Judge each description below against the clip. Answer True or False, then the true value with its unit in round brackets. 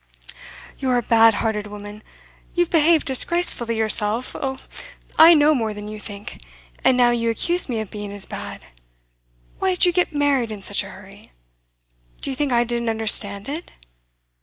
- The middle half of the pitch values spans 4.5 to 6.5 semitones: True (5.4 semitones)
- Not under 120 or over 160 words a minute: False (170 wpm)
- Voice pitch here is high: True (235 Hz)